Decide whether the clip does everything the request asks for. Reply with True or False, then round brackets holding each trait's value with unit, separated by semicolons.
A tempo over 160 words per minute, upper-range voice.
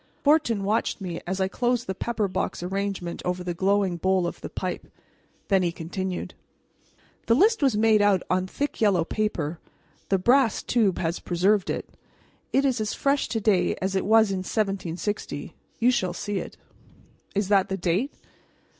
True (170 wpm; 195 Hz)